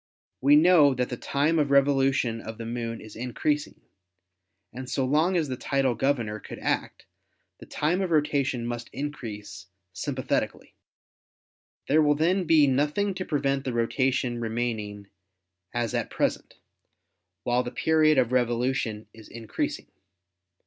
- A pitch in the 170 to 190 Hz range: No, low, 130 Hz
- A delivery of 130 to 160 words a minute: Yes, average, 140 wpm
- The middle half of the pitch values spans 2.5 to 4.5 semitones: Yes, average, 4.0 semitones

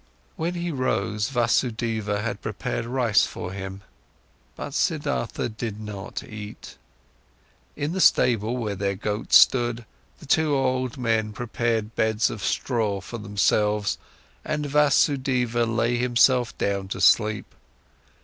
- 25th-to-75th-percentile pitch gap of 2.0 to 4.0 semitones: Yes, average, 3.2 semitones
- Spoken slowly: Yes, slow, 125 wpm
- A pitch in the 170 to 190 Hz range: No, low, 115 Hz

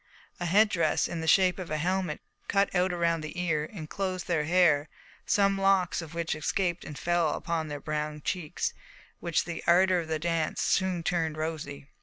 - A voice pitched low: No, medium, 170 Hz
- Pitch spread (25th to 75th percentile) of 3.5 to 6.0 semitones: No, average, 2.9 semitones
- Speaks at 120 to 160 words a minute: No, average, 185 wpm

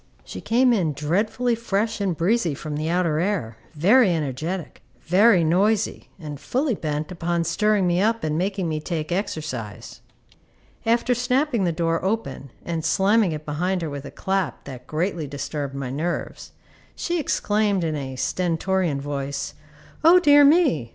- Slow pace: No, average, 155 wpm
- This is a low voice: No, medium, 175 Hz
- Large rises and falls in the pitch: Yes, wide, 5.7 semitones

